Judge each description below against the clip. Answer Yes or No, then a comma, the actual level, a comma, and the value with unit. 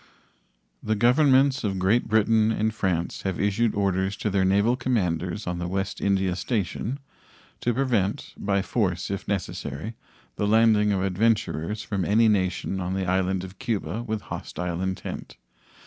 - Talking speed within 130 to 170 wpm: Yes, average, 150 wpm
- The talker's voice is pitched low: Yes, low, 100 Hz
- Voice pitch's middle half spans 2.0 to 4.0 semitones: Yes, average, 3.0 semitones